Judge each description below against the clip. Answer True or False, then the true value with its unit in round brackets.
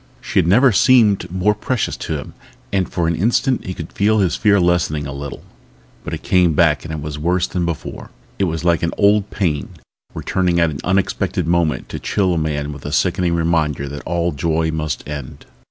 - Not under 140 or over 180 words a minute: False (200 wpm)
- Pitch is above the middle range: False (85 Hz)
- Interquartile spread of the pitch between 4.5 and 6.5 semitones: False (3.4 semitones)